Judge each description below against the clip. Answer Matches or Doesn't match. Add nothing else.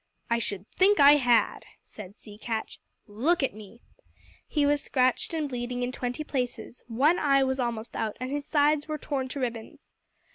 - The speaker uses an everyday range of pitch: Matches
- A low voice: Doesn't match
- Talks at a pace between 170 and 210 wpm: Matches